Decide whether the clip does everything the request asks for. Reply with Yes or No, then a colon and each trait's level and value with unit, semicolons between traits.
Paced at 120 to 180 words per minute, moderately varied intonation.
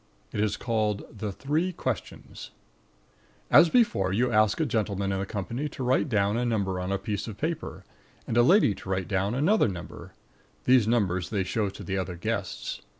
No: average, 190 wpm; average, 4.2 semitones